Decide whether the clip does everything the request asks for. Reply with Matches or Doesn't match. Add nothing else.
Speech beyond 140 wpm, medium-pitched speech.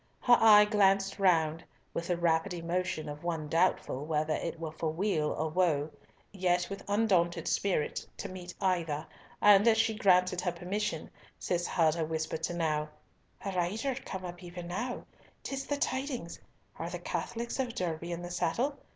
Matches